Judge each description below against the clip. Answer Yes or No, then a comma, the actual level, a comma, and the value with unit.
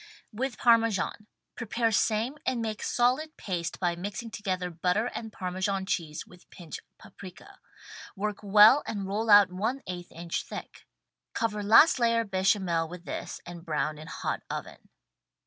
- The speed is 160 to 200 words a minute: No, average, 145 wpm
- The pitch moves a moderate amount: Yes, average, 4.1 semitones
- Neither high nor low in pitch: No, high, 205 Hz